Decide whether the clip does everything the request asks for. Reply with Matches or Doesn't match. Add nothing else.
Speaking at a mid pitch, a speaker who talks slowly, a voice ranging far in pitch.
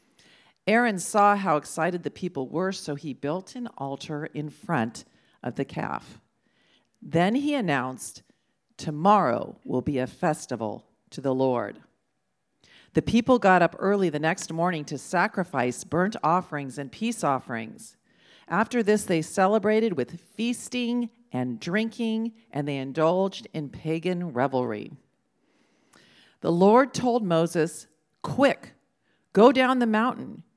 Matches